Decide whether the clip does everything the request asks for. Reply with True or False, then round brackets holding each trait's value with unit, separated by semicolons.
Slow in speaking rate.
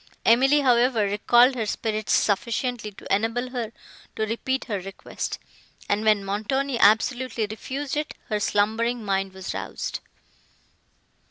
True (125 wpm)